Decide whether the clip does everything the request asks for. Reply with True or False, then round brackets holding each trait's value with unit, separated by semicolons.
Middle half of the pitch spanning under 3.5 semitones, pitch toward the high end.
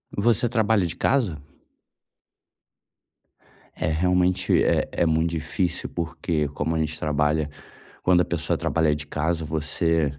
False (2.8 semitones; 80 Hz)